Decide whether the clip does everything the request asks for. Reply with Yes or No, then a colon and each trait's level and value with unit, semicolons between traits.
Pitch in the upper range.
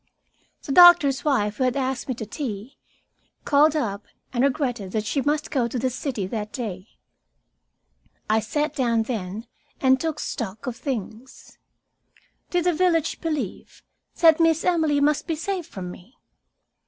Yes: very high, 260 Hz